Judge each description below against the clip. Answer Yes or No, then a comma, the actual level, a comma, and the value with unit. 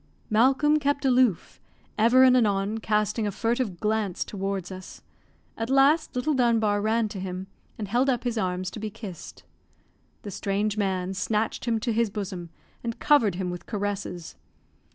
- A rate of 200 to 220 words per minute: No, average, 160 wpm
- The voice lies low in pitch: No, high, 215 Hz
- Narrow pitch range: No, average, 3.6 semitones